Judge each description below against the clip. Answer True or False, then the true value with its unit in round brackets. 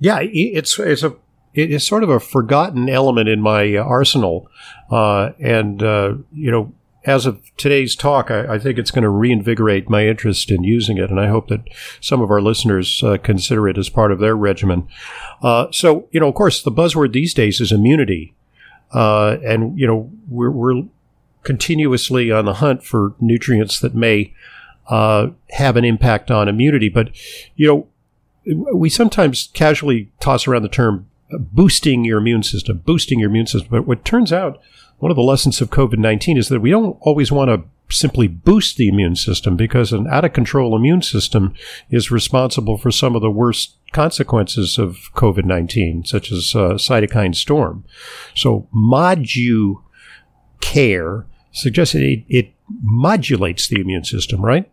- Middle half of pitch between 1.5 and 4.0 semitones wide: False (4.6 semitones)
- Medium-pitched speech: False (120 Hz)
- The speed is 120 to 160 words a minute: False (175 wpm)